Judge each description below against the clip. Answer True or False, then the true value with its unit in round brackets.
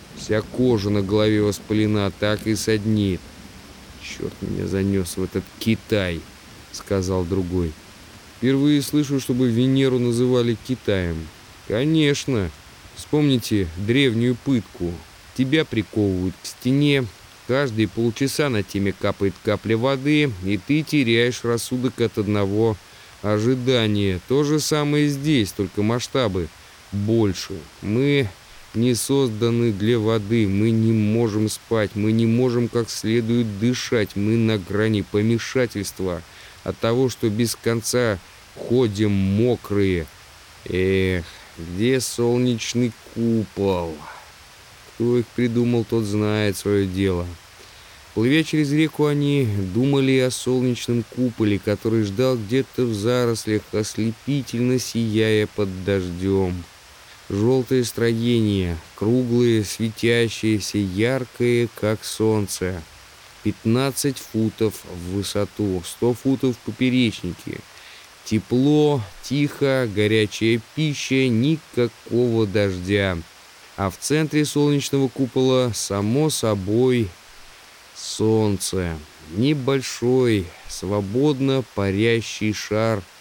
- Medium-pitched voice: False (110 Hz)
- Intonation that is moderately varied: True (4.0 semitones)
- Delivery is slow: True (100 wpm)